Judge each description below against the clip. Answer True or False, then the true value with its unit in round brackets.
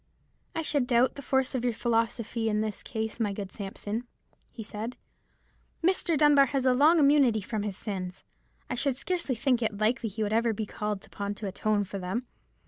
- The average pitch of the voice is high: True (230 Hz)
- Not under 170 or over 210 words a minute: True (200 wpm)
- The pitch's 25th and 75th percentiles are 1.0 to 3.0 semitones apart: False (3.8 semitones)